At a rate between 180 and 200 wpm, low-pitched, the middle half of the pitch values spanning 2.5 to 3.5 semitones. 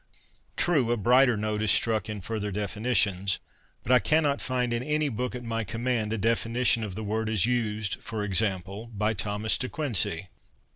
Yes: average, 185 wpm; low, 110 Hz; average, 2.9 semitones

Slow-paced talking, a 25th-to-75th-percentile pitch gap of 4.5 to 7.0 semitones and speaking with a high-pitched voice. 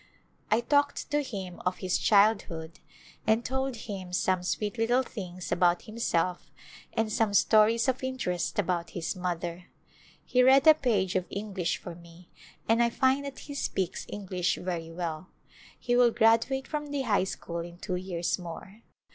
No: average, 165 wpm; average, 5.2 semitones; high, 200 Hz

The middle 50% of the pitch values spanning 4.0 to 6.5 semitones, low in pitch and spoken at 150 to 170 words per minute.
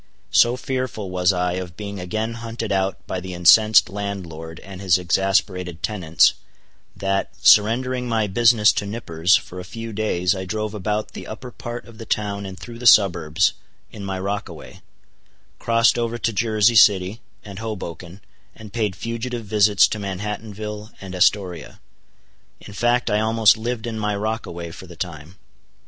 No: average, 3.3 semitones; low, 105 Hz; average, 160 wpm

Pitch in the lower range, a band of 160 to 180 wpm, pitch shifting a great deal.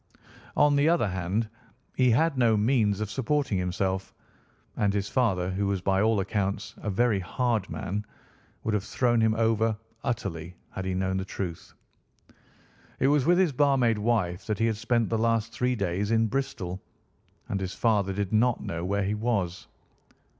No: low, 105 Hz; average, 175 wpm; average, 3.7 semitones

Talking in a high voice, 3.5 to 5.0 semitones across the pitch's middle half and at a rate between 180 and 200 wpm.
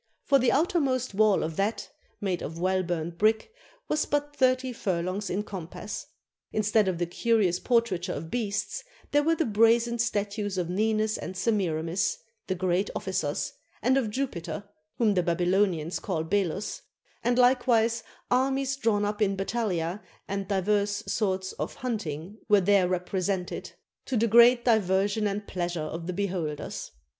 No: high, 205 Hz; average, 4.1 semitones; average, 155 wpm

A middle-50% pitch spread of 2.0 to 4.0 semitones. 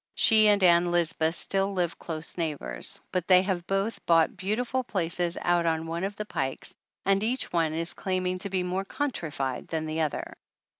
Yes: average, 3.0 semitones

